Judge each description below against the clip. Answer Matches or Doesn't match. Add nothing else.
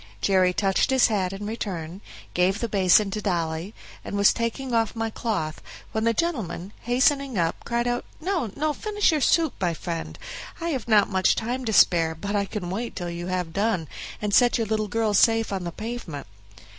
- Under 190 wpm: Doesn't match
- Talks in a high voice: Matches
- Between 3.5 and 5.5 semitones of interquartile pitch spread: Matches